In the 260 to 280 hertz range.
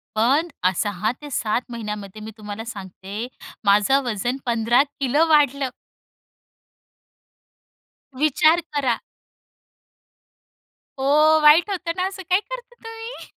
Yes: very high, 265 Hz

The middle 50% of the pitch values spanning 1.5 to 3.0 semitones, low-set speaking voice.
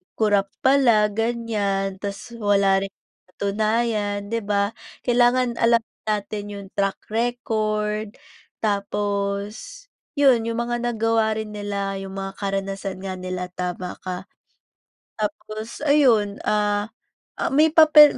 No: narrow, 2.6 semitones; high, 210 Hz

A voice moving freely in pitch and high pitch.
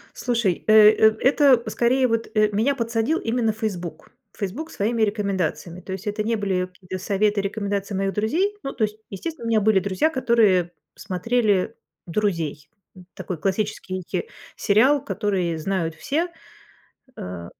No: average, 3.7 semitones; high, 210 Hz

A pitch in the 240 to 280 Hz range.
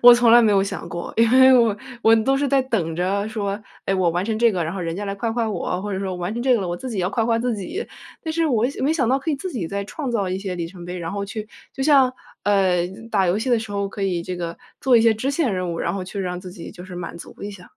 No: high, 205 Hz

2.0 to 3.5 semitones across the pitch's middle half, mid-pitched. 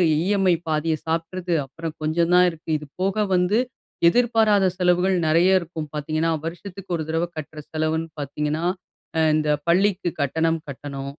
Yes: average, 2.8 semitones; medium, 165 Hz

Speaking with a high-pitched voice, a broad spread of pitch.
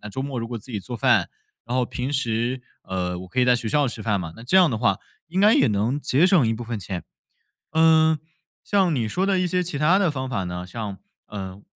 No: low, 125 Hz; wide, 6.8 semitones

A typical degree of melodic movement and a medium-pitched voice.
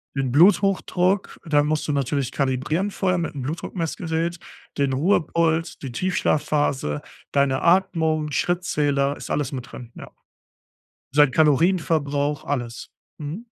Yes: average, 3.5 semitones; medium, 150 Hz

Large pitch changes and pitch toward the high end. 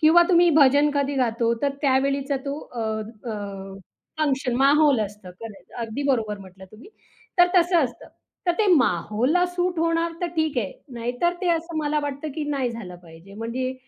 Yes: wide, 5.8 semitones; very high, 275 Hz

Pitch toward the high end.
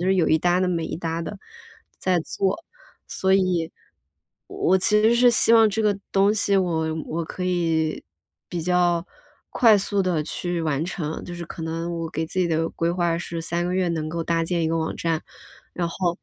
No: medium, 175 Hz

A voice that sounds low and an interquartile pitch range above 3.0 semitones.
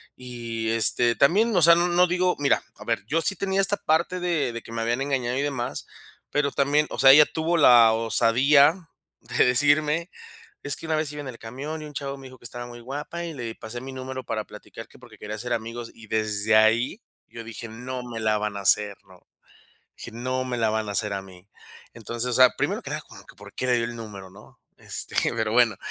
Yes: low, 125 Hz; average, 4.5 semitones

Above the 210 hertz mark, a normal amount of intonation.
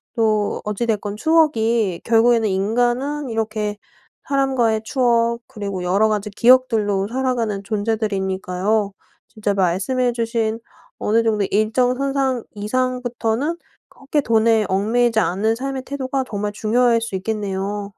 Yes: high, 225 Hz; average, 3.1 semitones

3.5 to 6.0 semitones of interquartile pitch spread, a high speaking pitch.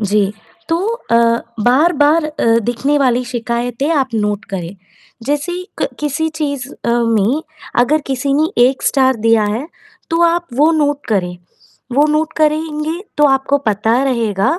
Yes: average, 4.7 semitones; very high, 270 Hz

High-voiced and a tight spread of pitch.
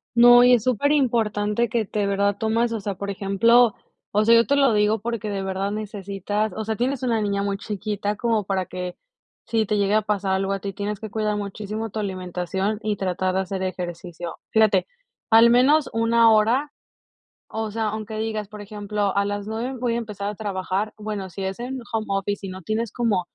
Yes: high, 210 Hz; narrow, 2.3 semitones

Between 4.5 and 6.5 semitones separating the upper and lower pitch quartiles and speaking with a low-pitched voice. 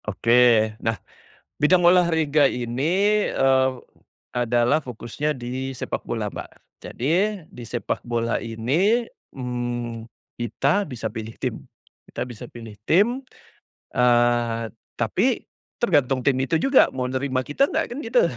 Yes: average, 5.1 semitones; low, 125 Hz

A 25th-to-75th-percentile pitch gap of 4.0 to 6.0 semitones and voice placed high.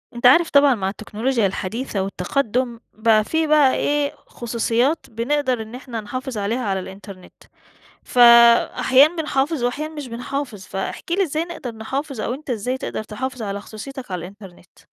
Yes: average, 4.7 semitones; high, 245 Hz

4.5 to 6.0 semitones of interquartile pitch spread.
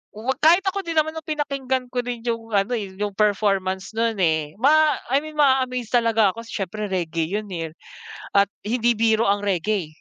Yes: average, 4.8 semitones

